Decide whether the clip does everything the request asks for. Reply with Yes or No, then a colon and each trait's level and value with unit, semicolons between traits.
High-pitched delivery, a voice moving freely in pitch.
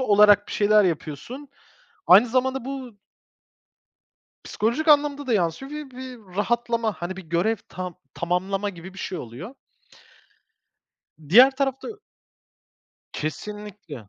Yes: high, 210 Hz; wide, 6.2 semitones